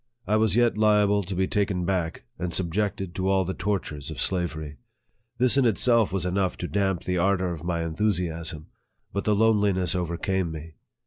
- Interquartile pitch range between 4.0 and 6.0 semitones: No, average, 3.1 semitones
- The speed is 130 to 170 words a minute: No, average, 185 wpm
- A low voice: Yes, very low, 95 Hz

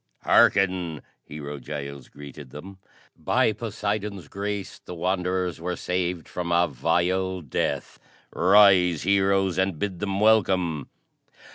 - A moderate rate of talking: No, slow, 115 wpm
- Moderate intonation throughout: Yes, average, 3.1 semitones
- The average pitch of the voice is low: Yes, very low, 90 Hz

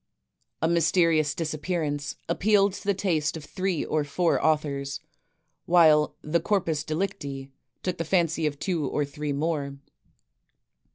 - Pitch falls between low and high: Yes, medium, 155 Hz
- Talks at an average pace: No, slow, 130 wpm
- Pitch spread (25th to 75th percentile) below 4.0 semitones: Yes, average, 2.9 semitones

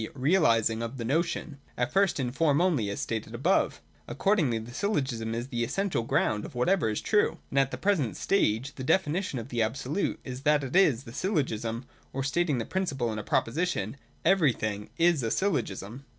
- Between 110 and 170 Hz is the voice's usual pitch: Yes, low, 135 Hz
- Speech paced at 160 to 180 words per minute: No, average, 190 wpm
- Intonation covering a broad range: Yes, wide, 6.8 semitones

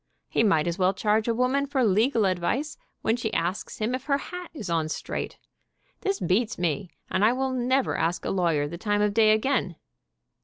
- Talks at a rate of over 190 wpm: Yes, average, 200 wpm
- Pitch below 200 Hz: No, high, 215 Hz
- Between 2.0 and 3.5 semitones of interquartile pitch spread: No, wide, 5.6 semitones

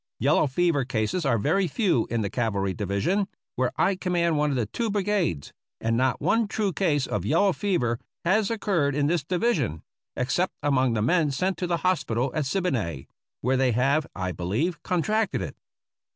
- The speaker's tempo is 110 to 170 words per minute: No, average, 180 wpm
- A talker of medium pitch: Yes, medium, 145 Hz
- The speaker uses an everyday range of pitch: No, wide, 7.5 semitones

